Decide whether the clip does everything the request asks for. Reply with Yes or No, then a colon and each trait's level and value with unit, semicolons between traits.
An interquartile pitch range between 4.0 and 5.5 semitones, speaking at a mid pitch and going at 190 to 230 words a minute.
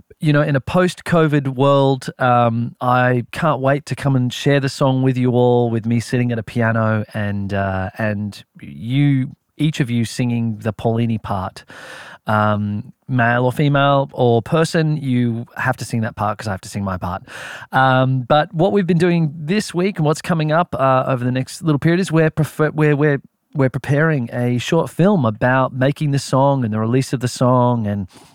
No: average, 4.3 semitones; low, 130 Hz; average, 200 wpm